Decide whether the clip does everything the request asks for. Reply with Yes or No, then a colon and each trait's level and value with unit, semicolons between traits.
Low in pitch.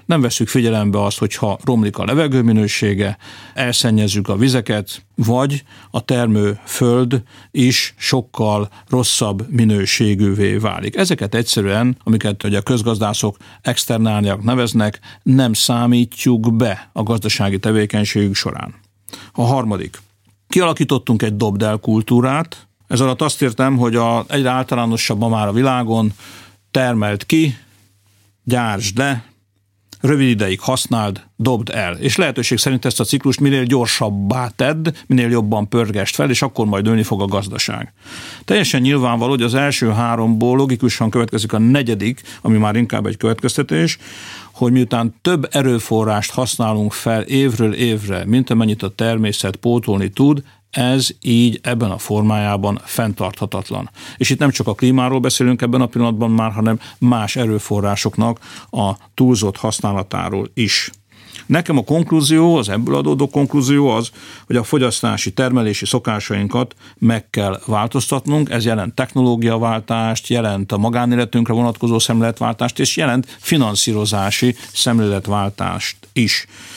Yes: low, 115 Hz